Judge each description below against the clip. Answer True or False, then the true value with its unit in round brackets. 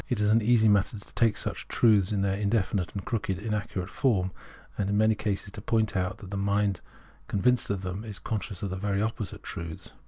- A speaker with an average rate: False (215 wpm)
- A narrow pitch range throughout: True (2.1 semitones)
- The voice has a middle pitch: False (100 Hz)